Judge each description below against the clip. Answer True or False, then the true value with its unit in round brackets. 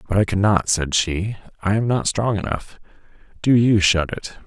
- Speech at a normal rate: True (190 wpm)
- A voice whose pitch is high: False (100 Hz)